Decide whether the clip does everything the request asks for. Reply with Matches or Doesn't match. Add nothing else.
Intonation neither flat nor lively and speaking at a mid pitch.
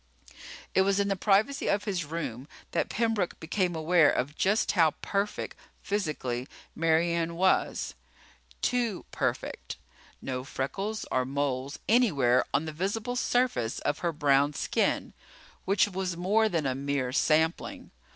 Doesn't match